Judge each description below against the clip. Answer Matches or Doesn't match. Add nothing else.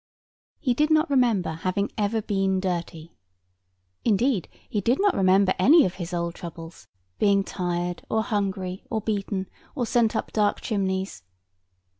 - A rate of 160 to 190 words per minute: Doesn't match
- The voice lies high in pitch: Matches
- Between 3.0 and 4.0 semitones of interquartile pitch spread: Matches